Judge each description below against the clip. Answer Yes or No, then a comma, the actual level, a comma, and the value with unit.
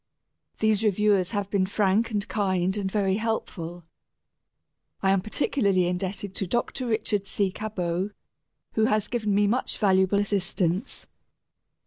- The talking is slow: Yes, slow, 130 wpm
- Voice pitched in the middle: No, high, 200 Hz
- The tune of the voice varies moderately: No, narrow, 2.2 semitones